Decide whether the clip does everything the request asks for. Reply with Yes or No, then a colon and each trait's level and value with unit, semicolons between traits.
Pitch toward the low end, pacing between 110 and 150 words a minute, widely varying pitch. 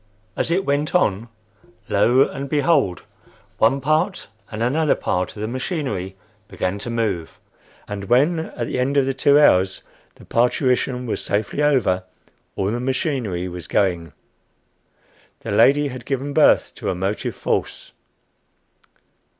Yes: low, 125 Hz; average, 140 wpm; wide, 6.1 semitones